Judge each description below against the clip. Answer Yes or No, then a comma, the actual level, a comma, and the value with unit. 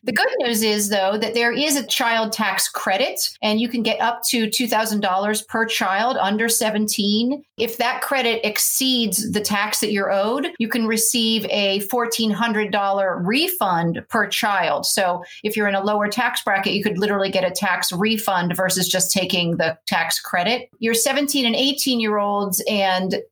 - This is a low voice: No, high, 215 Hz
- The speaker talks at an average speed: Yes, average, 175 wpm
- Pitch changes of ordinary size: Yes, average, 3.0 semitones